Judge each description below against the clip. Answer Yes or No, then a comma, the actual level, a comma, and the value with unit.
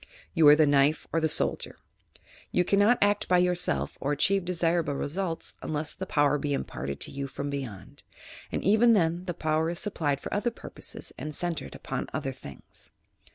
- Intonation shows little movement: No, average, 3.9 semitones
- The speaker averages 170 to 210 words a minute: Yes, average, 180 wpm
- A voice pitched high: No, medium, 160 Hz